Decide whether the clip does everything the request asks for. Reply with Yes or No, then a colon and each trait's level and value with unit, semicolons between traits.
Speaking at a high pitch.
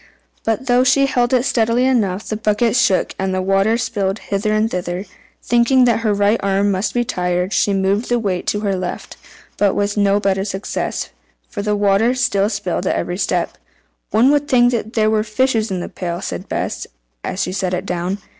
Yes: high, 205 Hz